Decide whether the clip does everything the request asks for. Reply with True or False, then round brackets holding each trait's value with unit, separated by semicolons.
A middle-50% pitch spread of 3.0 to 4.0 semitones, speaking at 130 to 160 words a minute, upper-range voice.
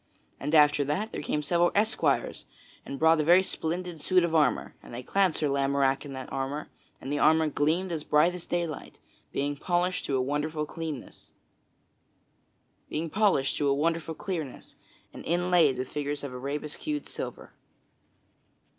False (3.5 semitones; 140 wpm; 155 Hz)